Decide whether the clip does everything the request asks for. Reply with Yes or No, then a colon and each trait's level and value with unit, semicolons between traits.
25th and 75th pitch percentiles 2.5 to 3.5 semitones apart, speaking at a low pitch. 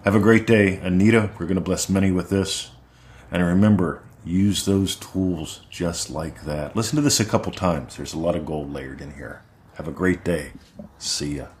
No: average, 4.1 semitones; very low, 95 Hz